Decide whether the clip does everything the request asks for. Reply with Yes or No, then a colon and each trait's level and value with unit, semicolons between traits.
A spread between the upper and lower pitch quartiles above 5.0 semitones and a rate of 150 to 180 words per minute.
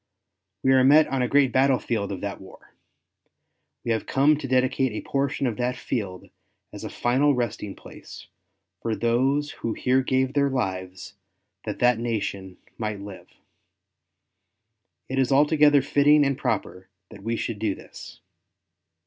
No: average, 4.2 semitones; average, 155 wpm